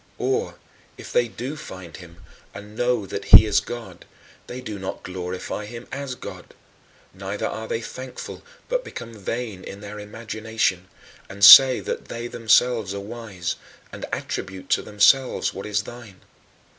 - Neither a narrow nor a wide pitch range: Yes, average, 3.6 semitones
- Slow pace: No, average, 155 wpm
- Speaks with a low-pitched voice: Yes, low, 110 Hz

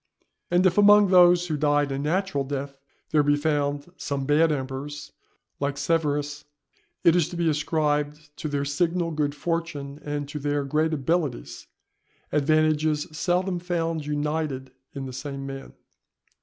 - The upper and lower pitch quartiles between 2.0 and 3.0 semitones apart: Yes, narrow, 2.6 semitones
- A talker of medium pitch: Yes, medium, 150 Hz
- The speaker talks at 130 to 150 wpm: Yes, average, 145 wpm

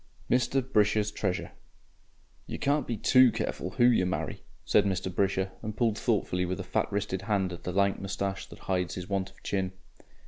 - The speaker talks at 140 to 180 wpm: No, average, 195 wpm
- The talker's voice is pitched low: Yes, low, 100 Hz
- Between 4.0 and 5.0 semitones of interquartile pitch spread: No, average, 2.7 semitones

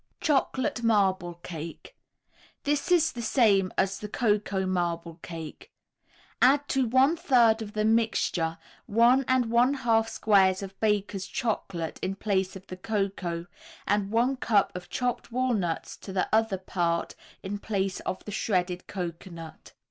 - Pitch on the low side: No, high, 205 Hz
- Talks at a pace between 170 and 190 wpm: No, average, 145 wpm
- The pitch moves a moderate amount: Yes, average, 4.2 semitones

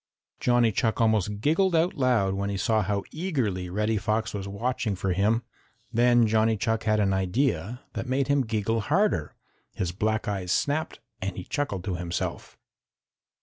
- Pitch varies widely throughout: No, average, 4.0 semitones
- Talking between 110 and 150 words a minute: No, average, 165 wpm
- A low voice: Yes, low, 110 Hz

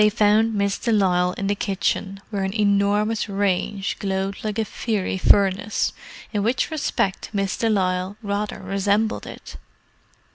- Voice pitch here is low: No, high, 200 Hz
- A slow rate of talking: No, average, 150 wpm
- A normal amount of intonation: No, narrow, 1.5 semitones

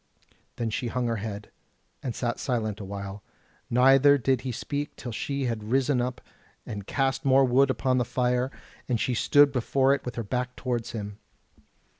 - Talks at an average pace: Yes, average, 180 wpm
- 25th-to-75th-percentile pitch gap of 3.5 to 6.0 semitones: No, average, 2.8 semitones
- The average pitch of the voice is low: Yes, low, 125 Hz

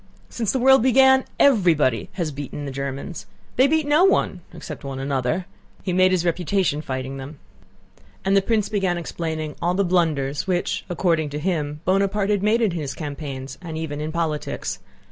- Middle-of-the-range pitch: Yes, medium, 170 Hz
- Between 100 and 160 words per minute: No, average, 170 wpm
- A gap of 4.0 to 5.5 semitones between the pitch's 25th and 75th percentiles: Yes, average, 5.2 semitones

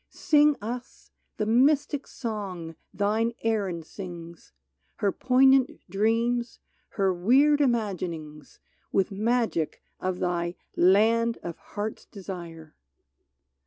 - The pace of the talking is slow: Yes, slow, 100 wpm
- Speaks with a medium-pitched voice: No, high, 210 Hz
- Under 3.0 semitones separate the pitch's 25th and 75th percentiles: No, average, 5.1 semitones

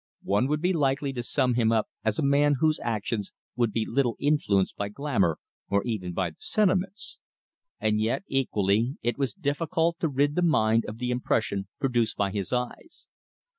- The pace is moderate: Yes, average, 180 wpm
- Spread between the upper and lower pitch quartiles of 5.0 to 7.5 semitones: Yes, average, 5.3 semitones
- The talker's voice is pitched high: No, low, 125 Hz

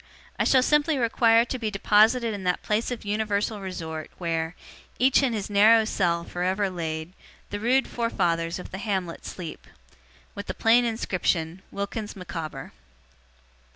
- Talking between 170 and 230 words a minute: No, average, 155 wpm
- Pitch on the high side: Yes, high, 200 Hz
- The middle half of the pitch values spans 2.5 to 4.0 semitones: No, average, 4.5 semitones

